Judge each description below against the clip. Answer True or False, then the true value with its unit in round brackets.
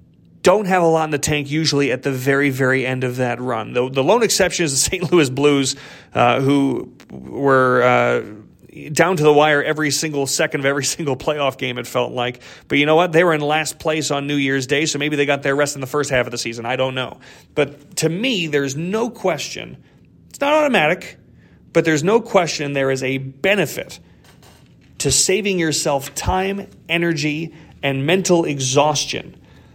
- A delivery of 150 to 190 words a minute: False (200 wpm)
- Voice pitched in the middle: True (145 Hz)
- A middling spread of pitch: True (3.3 semitones)